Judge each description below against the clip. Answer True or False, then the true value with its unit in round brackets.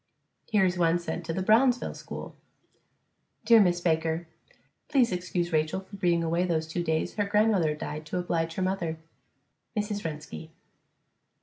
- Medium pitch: True (175 Hz)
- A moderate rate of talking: True (150 wpm)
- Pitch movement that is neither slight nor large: True (3.2 semitones)